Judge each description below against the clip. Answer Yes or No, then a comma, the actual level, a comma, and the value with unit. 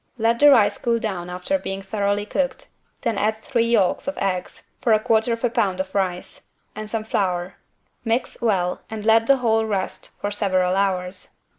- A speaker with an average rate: Yes, average, 170 wpm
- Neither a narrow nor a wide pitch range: Yes, average, 3.3 semitones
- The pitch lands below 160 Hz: No, high, 210 Hz